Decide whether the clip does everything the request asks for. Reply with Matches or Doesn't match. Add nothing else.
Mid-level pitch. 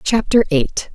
Doesn't match